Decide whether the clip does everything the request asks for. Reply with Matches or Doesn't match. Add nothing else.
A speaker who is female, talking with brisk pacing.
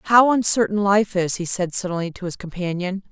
Doesn't match